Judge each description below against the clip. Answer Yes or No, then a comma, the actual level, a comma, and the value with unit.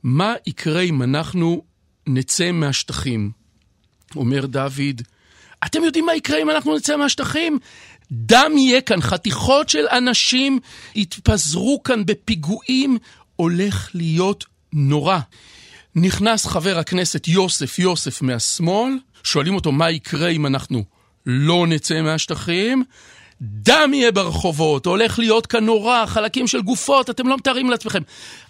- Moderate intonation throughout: No, wide, 8.5 semitones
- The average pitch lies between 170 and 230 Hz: Yes, medium, 180 Hz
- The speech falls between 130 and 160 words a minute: No, average, 120 wpm